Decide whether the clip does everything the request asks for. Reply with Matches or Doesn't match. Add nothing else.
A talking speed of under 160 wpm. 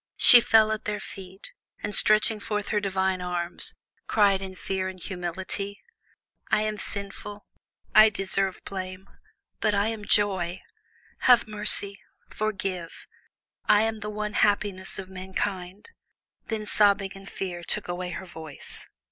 Matches